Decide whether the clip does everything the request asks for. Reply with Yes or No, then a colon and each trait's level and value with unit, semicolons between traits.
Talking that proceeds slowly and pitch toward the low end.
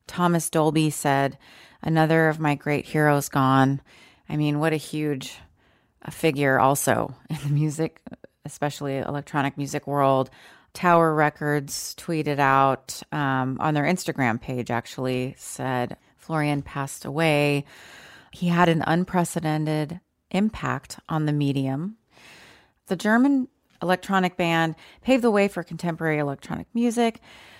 No: slow, 125 wpm; medium, 150 Hz